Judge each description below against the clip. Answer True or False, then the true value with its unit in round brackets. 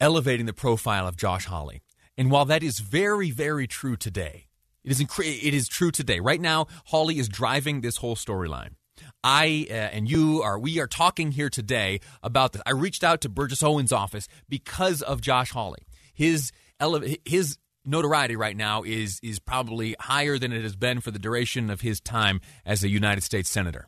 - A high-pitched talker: False (125 Hz)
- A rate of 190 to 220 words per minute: True (195 wpm)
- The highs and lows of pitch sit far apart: True (6.0 semitones)